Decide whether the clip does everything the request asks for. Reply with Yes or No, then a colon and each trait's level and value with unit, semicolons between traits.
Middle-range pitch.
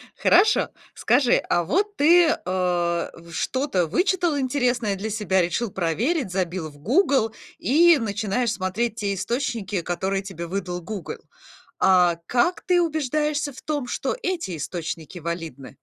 No: high, 210 Hz